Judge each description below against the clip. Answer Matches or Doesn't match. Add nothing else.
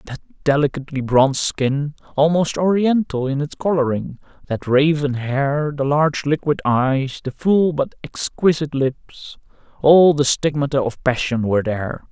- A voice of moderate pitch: Matches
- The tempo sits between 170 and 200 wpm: Doesn't match